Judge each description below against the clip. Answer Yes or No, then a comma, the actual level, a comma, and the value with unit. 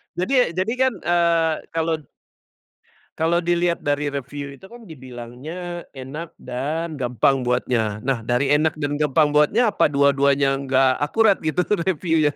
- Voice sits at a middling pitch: Yes, medium, 150 Hz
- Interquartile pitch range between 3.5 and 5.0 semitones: Yes, average, 4.0 semitones